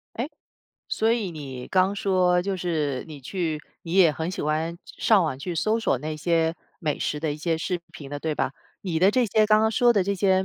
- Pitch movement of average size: Yes, average, 4.2 semitones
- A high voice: No, medium, 175 Hz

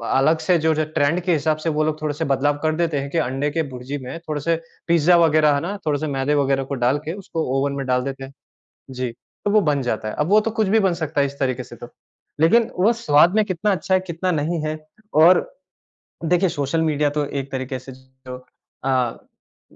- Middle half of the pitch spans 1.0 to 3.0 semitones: No, average, 3.7 semitones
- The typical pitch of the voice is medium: Yes, medium, 150 Hz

